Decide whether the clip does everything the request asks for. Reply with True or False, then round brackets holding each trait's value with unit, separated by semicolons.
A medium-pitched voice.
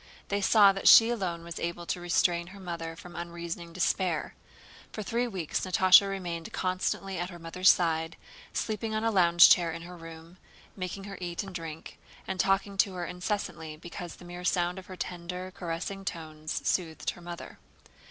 True (175 Hz)